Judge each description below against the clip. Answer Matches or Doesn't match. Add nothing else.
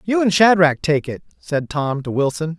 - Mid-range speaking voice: Matches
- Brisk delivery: Matches